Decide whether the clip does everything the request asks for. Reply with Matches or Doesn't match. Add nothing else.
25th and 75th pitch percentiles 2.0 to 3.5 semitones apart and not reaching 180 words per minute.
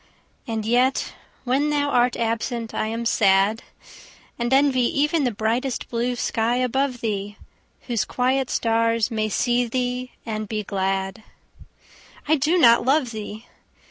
Matches